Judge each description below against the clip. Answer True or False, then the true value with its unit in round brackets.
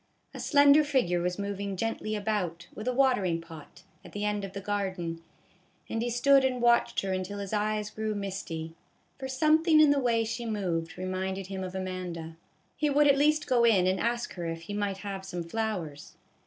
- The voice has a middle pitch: False (205 Hz)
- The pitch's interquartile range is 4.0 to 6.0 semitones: True (4.5 semitones)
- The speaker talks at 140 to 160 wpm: False (195 wpm)